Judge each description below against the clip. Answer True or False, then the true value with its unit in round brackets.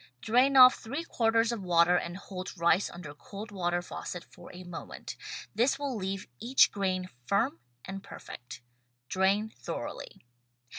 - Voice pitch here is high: True (195 Hz)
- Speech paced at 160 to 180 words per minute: False (145 wpm)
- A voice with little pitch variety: False (4.3 semitones)